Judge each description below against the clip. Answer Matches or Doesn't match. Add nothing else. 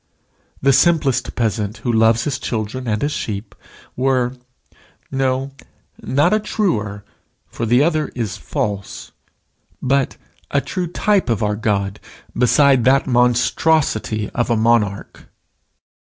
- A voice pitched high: Doesn't match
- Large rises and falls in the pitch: Doesn't match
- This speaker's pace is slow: Matches